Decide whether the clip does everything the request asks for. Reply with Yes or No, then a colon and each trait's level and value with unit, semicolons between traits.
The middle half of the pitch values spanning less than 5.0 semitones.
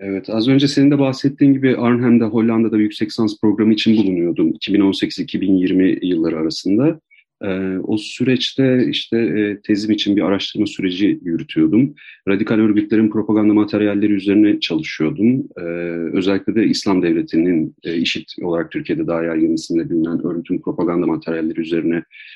Yes: average, 3.9 semitones